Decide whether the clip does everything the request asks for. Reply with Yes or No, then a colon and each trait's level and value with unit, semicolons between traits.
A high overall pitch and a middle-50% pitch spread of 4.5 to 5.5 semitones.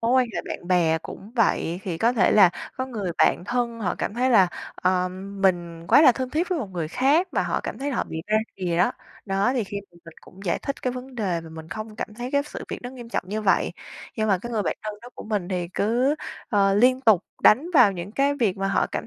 Yes: high, 210 Hz; average, 5.2 semitones